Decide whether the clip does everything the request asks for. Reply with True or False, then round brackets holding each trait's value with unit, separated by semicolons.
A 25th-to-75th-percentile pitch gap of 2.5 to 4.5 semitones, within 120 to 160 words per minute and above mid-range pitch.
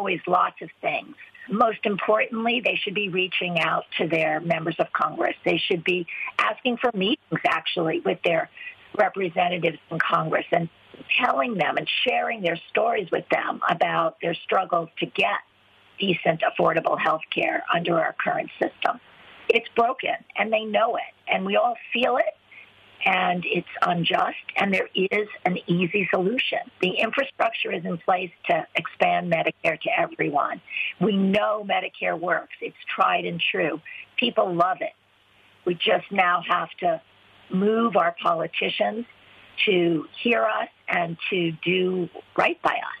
False (5.1 semitones; 150 wpm; 195 Hz)